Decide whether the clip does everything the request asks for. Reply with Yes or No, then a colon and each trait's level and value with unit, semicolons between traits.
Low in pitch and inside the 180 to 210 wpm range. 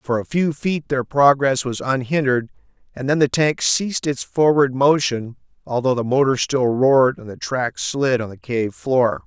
Yes: low, 130 Hz; average, 190 wpm